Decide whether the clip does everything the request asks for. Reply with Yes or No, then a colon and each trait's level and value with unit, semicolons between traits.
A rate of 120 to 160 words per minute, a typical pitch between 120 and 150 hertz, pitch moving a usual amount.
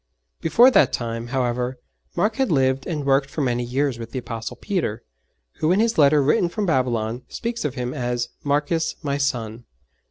No: average, 180 wpm; low, 135 Hz; average, 4.4 semitones